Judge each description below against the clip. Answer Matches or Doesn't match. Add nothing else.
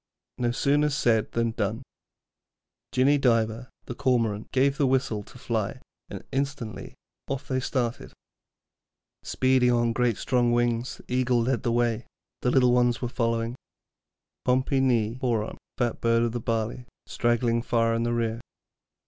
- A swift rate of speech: Doesn't match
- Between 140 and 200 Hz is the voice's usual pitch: Doesn't match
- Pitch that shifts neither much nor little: Doesn't match